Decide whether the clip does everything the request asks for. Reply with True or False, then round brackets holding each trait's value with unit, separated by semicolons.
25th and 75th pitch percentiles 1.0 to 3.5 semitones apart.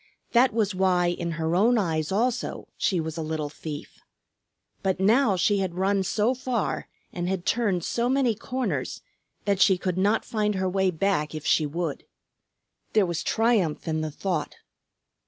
False (4.4 semitones)